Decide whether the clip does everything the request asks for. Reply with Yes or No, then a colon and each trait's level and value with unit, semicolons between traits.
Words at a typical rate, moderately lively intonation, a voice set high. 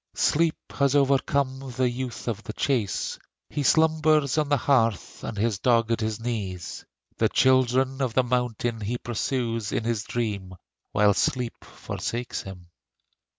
No: average, 150 wpm; average, 3.2 semitones; low, 120 Hz